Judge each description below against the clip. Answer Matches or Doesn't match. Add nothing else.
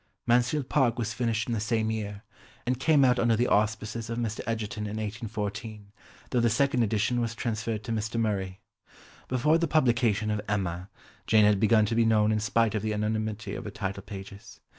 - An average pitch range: Doesn't match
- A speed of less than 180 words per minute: Doesn't match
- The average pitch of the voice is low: Matches